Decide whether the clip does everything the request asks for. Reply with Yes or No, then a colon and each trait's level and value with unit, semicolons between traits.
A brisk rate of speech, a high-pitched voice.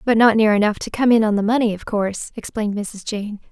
Yes: fast, 255 wpm; high, 215 Hz